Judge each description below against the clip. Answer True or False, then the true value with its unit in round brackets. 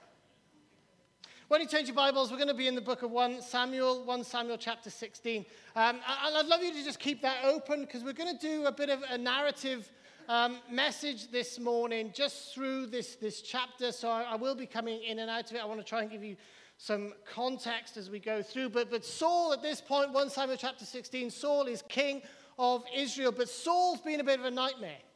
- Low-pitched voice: False (250 Hz)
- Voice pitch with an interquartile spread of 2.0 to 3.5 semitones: True (3.1 semitones)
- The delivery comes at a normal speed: False (225 wpm)